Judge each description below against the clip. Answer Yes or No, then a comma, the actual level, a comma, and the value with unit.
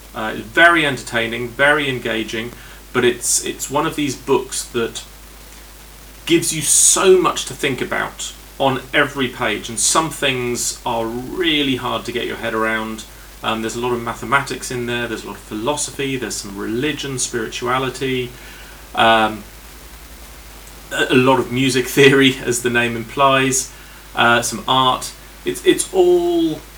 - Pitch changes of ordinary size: Yes, average, 3.3 semitones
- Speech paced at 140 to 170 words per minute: Yes, average, 150 wpm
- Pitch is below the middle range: Yes, low, 125 Hz